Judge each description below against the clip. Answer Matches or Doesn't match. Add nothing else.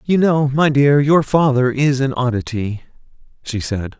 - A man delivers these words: Matches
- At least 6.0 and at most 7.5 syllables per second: Doesn't match